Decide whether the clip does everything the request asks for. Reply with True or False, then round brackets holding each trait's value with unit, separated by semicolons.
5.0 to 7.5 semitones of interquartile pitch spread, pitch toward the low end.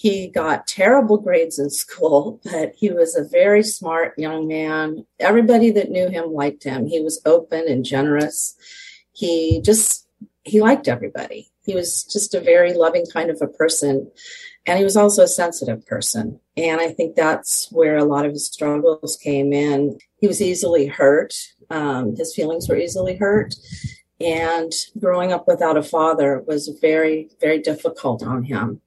False (5.3 semitones; 165 Hz)